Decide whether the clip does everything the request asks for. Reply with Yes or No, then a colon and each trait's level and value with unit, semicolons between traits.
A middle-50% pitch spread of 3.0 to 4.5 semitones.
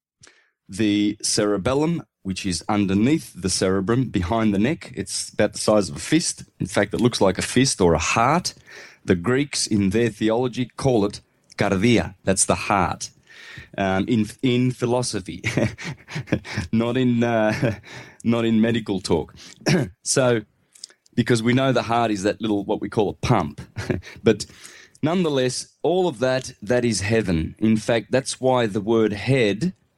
Yes: average, 3.4 semitones